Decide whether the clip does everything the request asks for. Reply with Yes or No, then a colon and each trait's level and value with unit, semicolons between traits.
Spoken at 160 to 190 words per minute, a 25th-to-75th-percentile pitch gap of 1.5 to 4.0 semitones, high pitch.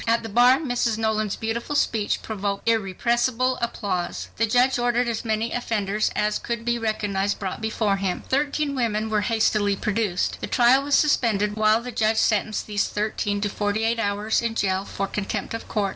Yes: average, 180 wpm; narrow, 2.4 semitones; high, 220 Hz